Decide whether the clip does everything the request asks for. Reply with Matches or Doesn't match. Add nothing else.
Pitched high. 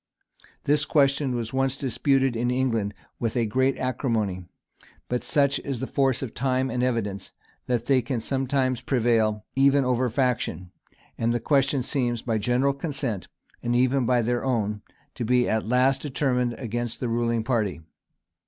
Doesn't match